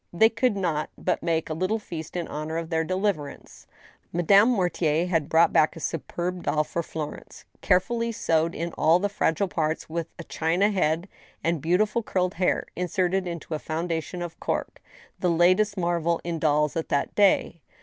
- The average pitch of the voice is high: No, medium, 170 Hz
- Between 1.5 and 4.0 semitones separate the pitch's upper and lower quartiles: Yes, narrow, 2.5 semitones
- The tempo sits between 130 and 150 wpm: No, average, 180 wpm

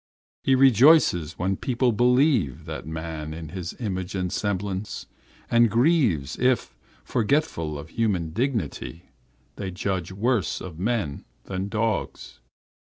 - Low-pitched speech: Yes, low, 100 Hz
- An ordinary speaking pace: No, slow, 125 wpm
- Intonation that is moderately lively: No, wide, 6.3 semitones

